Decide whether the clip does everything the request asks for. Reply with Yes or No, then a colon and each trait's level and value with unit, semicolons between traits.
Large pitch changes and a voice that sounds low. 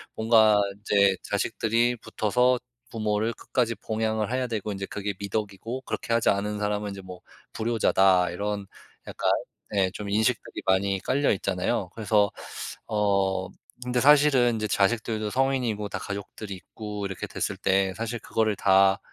No: narrow, 2.6 semitones; low, 105 Hz